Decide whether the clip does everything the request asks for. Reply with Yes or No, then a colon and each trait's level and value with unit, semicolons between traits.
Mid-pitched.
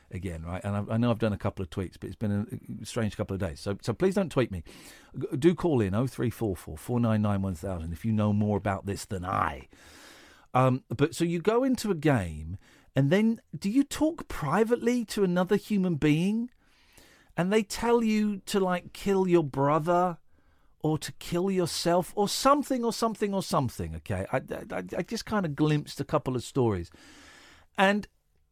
Yes: medium, 145 Hz